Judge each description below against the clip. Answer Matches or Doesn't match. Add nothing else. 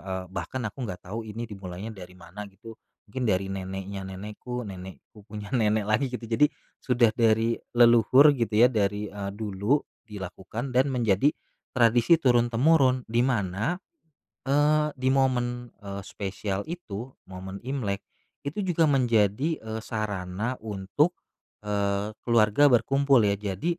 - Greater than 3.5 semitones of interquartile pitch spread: Matches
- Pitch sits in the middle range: Doesn't match